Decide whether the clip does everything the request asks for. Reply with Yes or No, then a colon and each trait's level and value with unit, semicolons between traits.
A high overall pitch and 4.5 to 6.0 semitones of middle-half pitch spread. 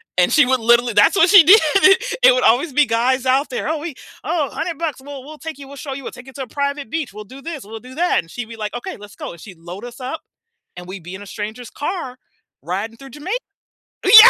Yes: very high, 260 Hz; average, 5.3 semitones